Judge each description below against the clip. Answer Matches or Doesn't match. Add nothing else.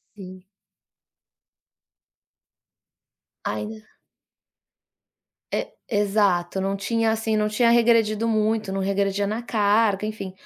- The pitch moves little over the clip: Matches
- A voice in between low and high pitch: Doesn't match